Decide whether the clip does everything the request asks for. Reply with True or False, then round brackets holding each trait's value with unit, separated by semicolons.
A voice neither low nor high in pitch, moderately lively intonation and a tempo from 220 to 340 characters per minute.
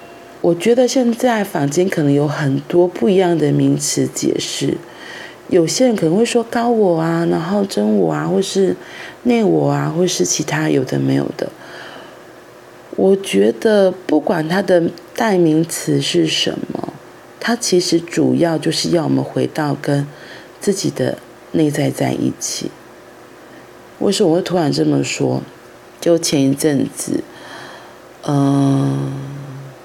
False (165 Hz; 5.0 semitones; 200 characters per minute)